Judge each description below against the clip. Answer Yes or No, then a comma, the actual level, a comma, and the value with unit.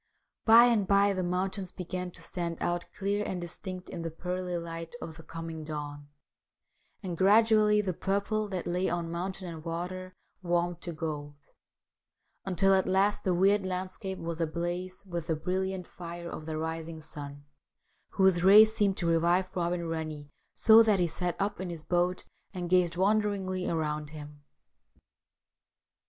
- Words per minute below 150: No, average, 160 wpm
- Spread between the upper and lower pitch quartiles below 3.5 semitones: Yes, narrow, 2.4 semitones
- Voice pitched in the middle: Yes, medium, 180 Hz